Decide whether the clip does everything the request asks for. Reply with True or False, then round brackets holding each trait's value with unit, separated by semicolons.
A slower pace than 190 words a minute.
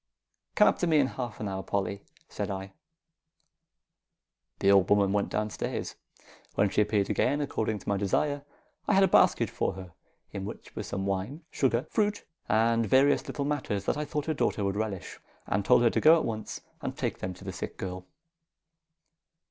False (195 wpm)